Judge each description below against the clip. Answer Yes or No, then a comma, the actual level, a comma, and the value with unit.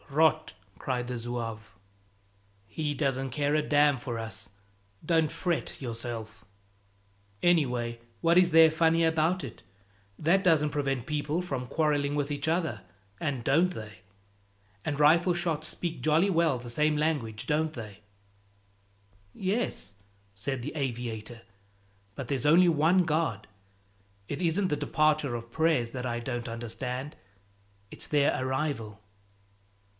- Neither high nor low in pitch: Yes, medium, 145 Hz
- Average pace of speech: No, slow, 130 wpm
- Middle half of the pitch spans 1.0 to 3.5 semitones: No, average, 5.0 semitones